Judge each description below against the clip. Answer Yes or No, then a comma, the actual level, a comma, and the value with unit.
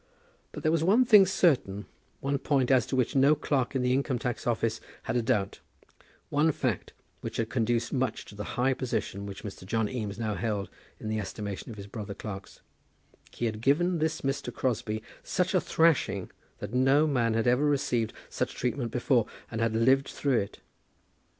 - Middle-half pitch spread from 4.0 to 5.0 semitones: Yes, average, 4.3 semitones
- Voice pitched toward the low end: Yes, low, 125 Hz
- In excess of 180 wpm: Yes, average, 190 wpm